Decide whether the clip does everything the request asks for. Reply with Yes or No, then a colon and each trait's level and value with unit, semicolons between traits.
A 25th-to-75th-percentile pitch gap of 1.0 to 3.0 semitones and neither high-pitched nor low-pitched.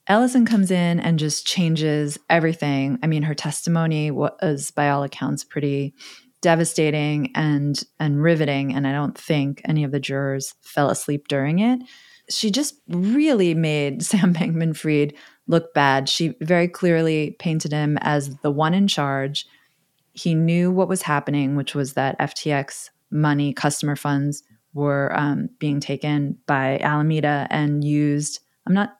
Yes: average, 2.7 semitones; medium, 150 Hz